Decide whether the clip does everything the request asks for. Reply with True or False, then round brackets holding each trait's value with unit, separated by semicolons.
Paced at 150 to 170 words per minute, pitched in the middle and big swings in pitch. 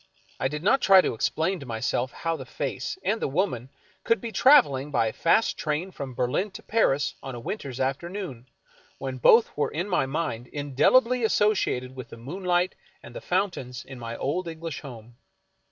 False (190 wpm; 150 Hz; 6.6 semitones)